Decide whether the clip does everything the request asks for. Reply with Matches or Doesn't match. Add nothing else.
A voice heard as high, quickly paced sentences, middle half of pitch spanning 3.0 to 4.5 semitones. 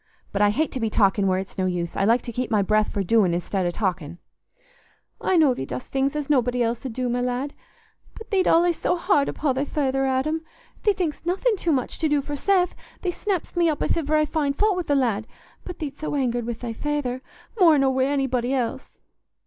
Doesn't match